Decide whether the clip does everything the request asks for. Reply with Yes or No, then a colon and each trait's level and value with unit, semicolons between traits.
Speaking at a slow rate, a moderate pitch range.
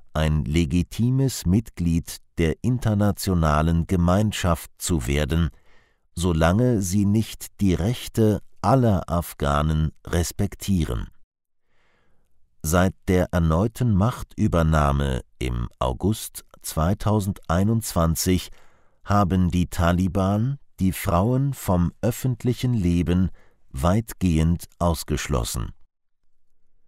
Yes: slow, 75 wpm; average, 4.4 semitones